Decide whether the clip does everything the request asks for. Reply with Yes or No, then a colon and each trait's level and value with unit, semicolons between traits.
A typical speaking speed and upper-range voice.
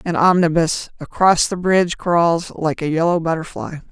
No: average, 155 wpm; medium, 170 Hz